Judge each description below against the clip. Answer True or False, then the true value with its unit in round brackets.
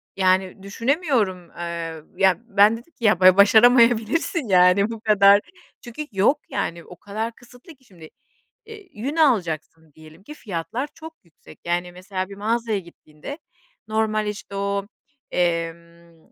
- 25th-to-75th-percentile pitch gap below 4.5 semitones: False (5.0 semitones)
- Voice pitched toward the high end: True (200 Hz)